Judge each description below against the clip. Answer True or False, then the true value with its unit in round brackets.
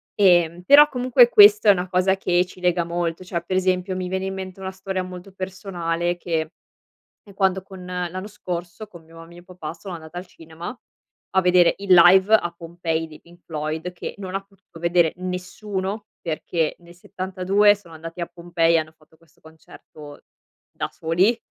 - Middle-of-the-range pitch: True (180 Hz)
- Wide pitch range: False (2.1 semitones)